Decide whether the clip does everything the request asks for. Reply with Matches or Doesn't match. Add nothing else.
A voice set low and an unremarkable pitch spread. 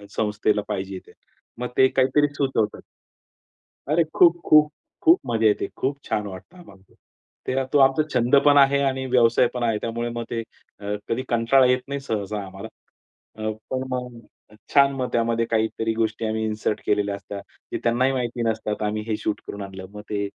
Matches